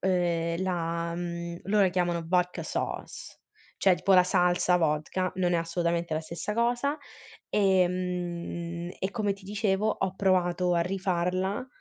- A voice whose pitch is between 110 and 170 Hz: No, medium, 180 Hz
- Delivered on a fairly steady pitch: Yes, narrow, 1.9 semitones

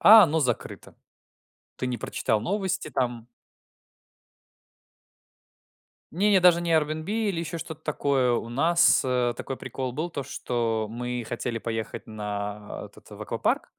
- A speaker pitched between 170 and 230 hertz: No, low, 130 Hz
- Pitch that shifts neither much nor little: No, wide, 5.9 semitones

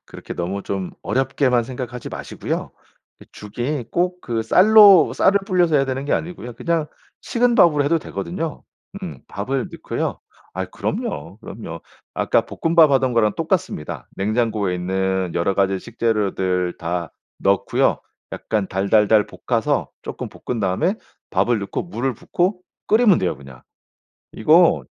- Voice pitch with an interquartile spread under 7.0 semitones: No, wide, 8.5 semitones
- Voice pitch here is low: Yes, low, 115 Hz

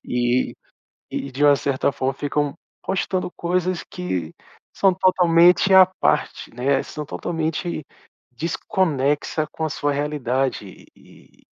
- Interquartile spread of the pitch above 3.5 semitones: Yes, average, 4.5 semitones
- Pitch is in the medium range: Yes, medium, 150 Hz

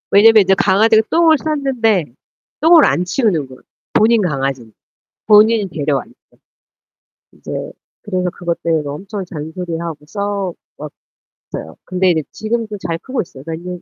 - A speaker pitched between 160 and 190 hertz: Yes, medium, 185 Hz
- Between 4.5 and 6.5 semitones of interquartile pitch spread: Yes, average, 5.1 semitones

